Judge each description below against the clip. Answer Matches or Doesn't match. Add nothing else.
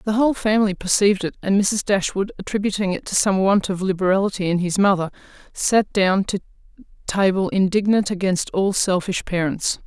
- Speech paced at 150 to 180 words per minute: Matches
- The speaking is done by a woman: Matches